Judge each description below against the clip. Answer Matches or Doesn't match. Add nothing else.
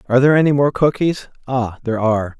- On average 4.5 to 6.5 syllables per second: Doesn't match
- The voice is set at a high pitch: Doesn't match